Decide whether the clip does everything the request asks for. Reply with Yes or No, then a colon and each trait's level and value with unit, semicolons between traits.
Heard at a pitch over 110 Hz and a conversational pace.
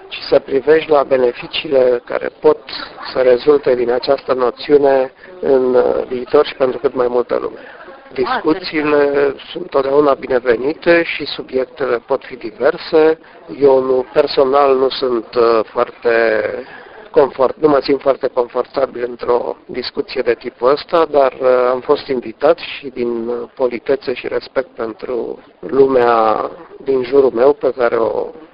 No: medium, 140 Hz; slow, 130 wpm